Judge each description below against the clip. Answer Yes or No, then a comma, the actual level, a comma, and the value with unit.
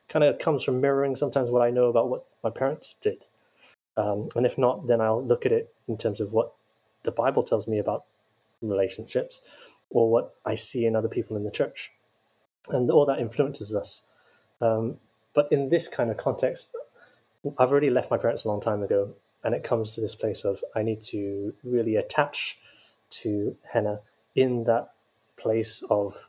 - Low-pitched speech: Yes, low, 120 Hz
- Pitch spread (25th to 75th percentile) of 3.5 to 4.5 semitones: Yes, average, 3.9 semitones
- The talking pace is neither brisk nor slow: Yes, average, 185 wpm